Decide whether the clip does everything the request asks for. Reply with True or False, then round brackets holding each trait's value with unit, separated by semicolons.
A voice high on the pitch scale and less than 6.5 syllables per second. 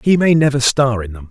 False (130 Hz; 5.8 syllables/s)